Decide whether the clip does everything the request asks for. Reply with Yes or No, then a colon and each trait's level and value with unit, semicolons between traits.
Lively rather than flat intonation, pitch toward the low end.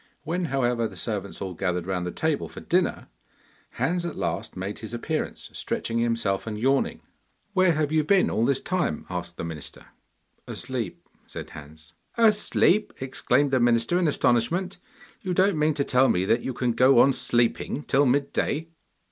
Yes: wide, 6.8 semitones; low, 130 Hz